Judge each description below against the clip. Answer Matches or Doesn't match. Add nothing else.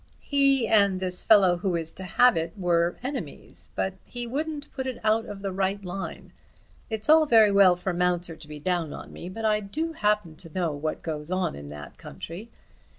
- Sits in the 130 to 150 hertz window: Doesn't match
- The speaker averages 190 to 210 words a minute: Matches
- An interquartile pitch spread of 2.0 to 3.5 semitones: Doesn't match